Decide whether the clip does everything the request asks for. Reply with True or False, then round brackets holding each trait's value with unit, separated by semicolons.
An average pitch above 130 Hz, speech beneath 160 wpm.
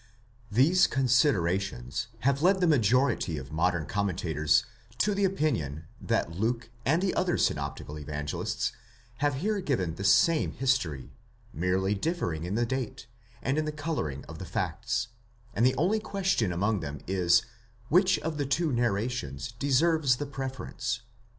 False (120 Hz; 150 wpm)